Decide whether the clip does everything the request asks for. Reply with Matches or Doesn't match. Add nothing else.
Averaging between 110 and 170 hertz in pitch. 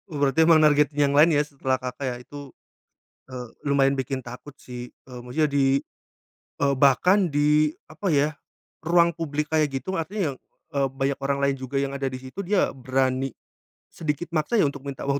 Matches